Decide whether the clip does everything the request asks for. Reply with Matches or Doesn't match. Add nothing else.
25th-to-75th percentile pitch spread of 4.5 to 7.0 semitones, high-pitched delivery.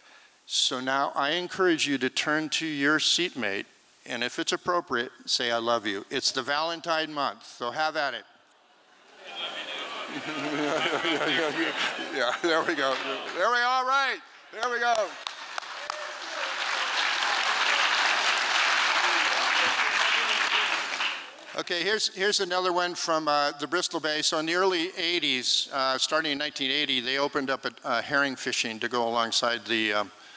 Doesn't match